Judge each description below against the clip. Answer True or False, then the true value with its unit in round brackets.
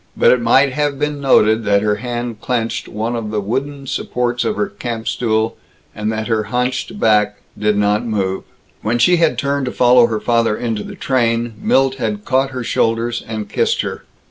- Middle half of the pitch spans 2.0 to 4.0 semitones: True (3.1 semitones)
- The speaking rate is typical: True (195 wpm)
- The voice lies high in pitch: False (115 Hz)